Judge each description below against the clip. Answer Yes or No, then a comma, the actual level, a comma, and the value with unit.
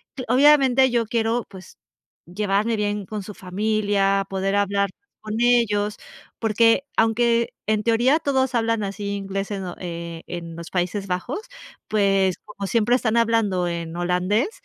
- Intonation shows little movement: No, average, 3.2 semitones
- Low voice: No, high, 210 Hz